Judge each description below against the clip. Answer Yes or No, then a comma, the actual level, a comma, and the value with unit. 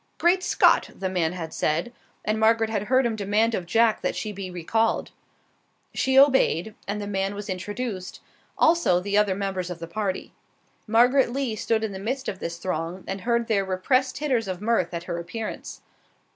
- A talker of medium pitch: No, high, 205 Hz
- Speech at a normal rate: Yes, average, 185 wpm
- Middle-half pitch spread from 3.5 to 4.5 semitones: Yes, average, 3.9 semitones